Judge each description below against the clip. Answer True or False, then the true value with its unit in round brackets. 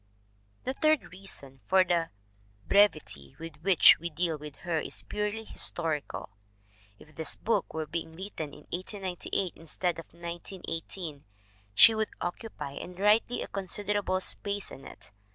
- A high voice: False (175 Hz)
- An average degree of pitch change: True (4.1 semitones)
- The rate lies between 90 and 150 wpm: True (145 wpm)